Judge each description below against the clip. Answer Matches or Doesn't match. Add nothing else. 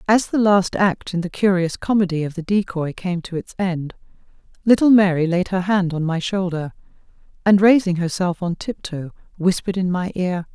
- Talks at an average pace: Matches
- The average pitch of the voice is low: Doesn't match